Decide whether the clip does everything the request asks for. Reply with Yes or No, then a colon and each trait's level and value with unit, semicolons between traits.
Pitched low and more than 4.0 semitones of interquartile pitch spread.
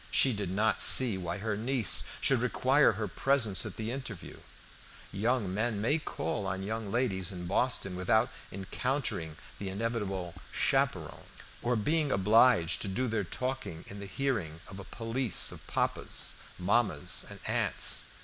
Yes: low, 110 Hz; average, 4.6 semitones